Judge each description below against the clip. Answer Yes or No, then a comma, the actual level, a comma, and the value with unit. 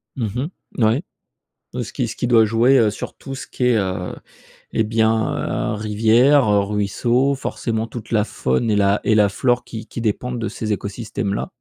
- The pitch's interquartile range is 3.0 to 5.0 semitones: No, narrow, 2.6 semitones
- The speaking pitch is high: No, low, 110 Hz